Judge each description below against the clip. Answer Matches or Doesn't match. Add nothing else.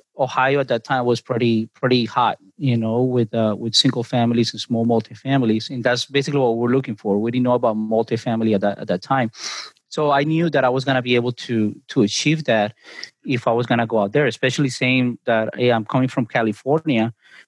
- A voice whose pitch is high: Doesn't match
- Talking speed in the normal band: Doesn't match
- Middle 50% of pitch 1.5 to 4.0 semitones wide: Matches